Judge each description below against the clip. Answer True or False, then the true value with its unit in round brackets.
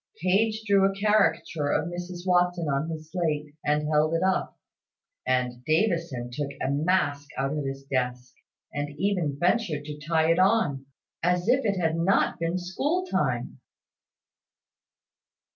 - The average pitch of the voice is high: False (165 Hz)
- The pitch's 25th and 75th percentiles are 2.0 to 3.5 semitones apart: False (4.2 semitones)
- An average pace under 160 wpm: True (145 wpm)